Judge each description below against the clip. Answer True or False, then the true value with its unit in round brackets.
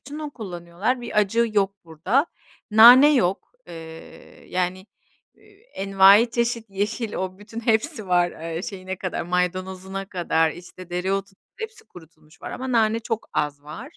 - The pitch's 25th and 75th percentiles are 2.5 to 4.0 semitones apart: False (4.5 semitones)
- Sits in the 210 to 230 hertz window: False (195 Hz)